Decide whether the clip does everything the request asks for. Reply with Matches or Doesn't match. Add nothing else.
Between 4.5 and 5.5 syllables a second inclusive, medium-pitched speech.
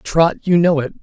Matches